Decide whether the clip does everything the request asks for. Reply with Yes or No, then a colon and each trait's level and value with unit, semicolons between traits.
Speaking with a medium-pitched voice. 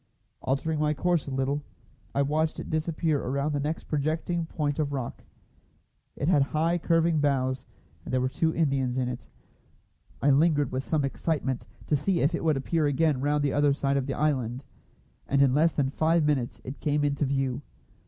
Yes: medium, 145 Hz